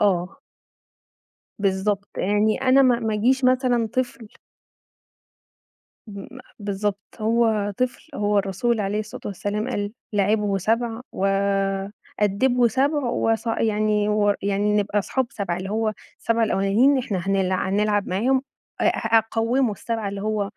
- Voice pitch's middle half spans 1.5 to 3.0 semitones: Yes, average, 2.7 semitones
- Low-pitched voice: No, high, 210 Hz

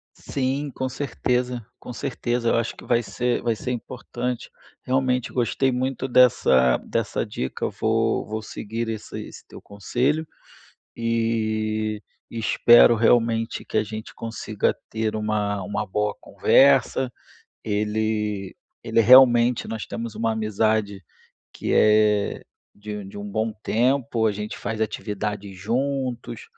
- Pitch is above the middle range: No, low, 115 Hz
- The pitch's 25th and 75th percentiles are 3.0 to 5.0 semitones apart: No, narrow, 2.6 semitones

